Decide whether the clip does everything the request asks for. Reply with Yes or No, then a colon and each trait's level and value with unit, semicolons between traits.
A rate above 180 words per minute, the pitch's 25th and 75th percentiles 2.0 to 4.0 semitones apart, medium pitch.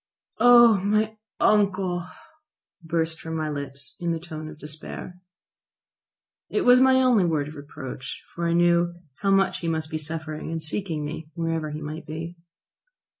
No: average, 160 wpm; average, 3.5 semitones; medium, 165 Hz